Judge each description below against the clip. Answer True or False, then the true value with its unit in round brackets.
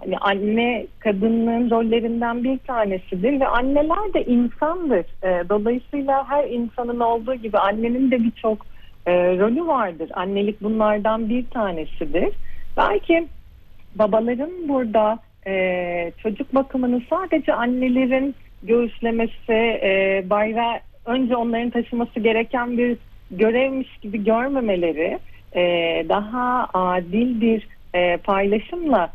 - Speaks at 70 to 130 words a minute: True (105 wpm)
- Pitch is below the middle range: False (230 Hz)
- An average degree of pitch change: True (3.6 semitones)